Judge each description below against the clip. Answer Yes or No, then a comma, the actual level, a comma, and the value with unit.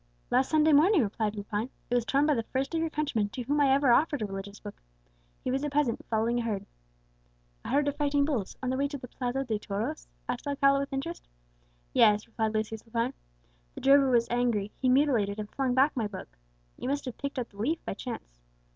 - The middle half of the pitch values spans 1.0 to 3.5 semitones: No, average, 4.4 semitones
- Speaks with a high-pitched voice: Yes, very high, 250 Hz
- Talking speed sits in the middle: No, fast, 225 wpm